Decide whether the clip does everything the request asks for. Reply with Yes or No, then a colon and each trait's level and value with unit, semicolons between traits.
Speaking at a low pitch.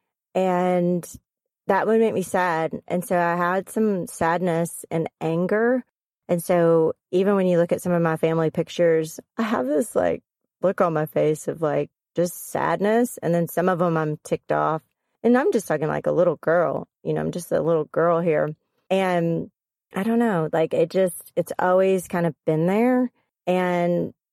No: medium, 175 Hz